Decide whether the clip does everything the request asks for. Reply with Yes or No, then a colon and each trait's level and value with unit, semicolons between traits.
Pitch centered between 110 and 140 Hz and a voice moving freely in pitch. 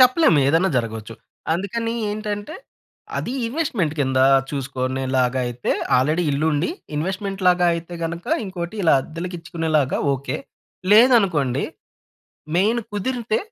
No: medium, 170 Hz; wide, 7.0 semitones